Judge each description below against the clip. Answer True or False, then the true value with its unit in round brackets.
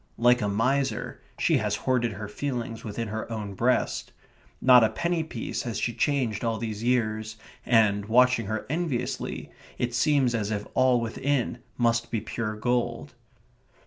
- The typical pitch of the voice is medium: False (115 Hz)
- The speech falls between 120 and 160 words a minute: True (155 wpm)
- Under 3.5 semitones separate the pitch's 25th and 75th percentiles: True (2.5 semitones)